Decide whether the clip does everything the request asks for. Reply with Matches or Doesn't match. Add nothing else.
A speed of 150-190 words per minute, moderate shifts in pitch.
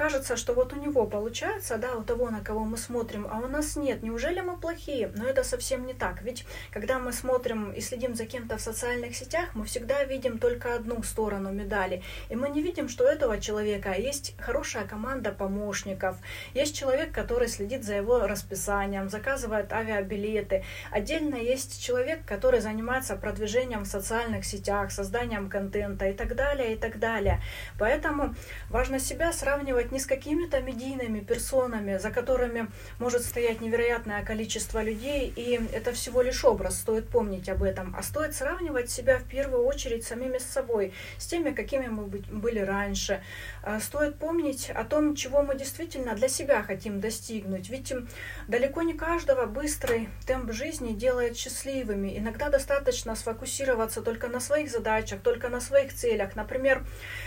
Matches